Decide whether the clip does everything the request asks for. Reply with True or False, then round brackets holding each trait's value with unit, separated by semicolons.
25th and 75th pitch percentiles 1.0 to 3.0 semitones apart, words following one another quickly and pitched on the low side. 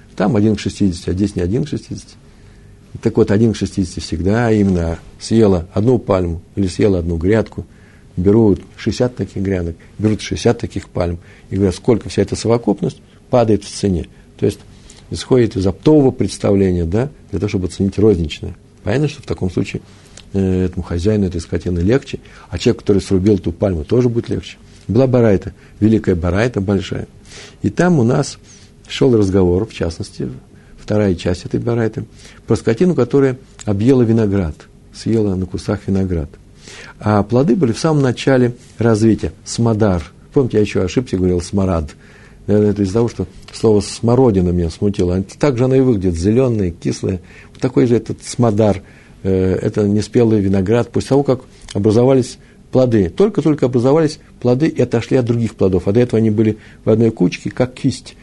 False (3.5 semitones; 165 wpm; 105 Hz)